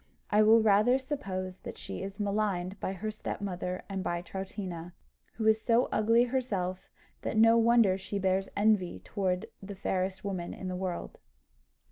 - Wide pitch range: No, average, 2.7 semitones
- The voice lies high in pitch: Yes, high, 195 Hz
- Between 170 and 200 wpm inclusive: No, average, 160 wpm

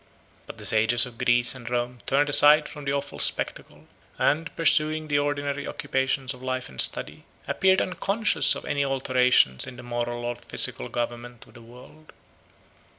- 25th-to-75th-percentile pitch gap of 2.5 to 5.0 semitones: Yes, average, 3.3 semitones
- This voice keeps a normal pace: Yes, average, 165 wpm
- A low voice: Yes, low, 130 Hz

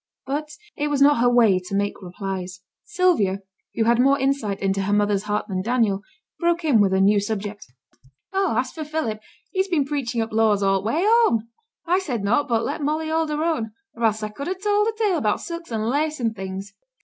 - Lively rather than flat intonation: Yes, wide, 7.1 semitones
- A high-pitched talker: Yes, high, 235 Hz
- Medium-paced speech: No, fast, 220 wpm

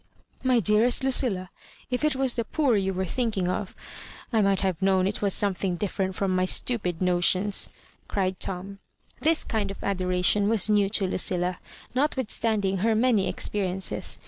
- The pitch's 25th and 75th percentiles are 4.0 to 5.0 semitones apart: No, average, 3.4 semitones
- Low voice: No, high, 200 Hz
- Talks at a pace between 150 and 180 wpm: Yes, average, 170 wpm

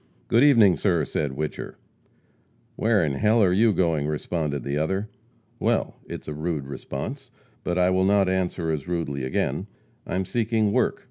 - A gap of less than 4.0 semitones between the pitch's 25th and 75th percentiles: No, average, 5.1 semitones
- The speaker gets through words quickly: No, average, 175 wpm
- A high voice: No, very low, 90 Hz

